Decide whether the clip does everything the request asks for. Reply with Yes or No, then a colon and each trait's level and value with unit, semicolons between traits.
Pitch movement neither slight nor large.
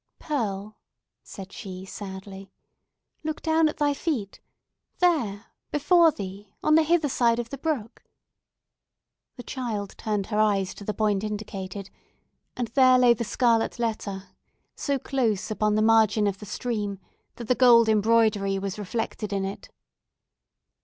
Yes: average, 4.0 semitones